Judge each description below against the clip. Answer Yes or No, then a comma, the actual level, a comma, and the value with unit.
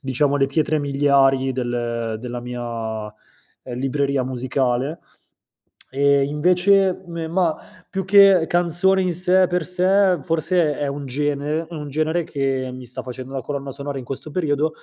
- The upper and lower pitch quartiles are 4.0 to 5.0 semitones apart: Yes, average, 4.5 semitones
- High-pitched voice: No, medium, 145 Hz